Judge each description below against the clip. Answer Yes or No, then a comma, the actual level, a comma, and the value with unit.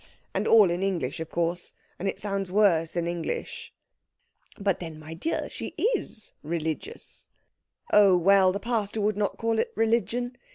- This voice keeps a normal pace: Yes, average, 160 wpm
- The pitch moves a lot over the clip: No, average, 4.1 semitones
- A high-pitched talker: Yes, high, 195 Hz